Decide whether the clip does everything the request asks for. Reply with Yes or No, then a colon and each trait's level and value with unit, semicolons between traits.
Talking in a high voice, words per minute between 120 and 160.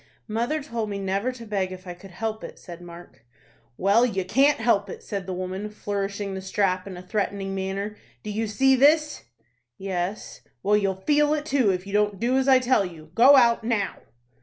No: high, 205 Hz; fast, 205 wpm